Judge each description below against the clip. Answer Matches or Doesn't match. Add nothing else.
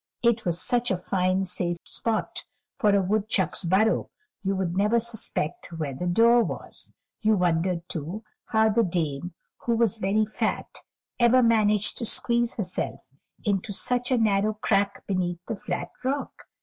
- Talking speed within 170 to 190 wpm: Doesn't match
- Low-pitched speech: Doesn't match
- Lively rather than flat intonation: Doesn't match